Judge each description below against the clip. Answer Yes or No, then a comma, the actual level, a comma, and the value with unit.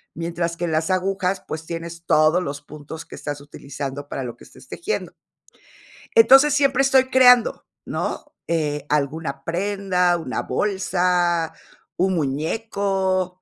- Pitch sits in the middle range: Yes, medium, 175 Hz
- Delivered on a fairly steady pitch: No, average, 4.1 semitones